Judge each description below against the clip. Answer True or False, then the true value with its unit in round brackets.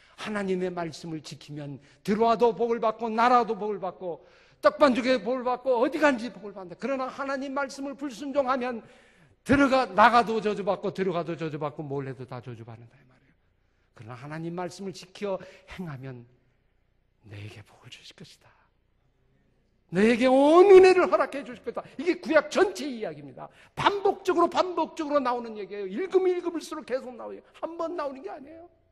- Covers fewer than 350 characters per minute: False (365 characters per minute)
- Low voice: False (230 Hz)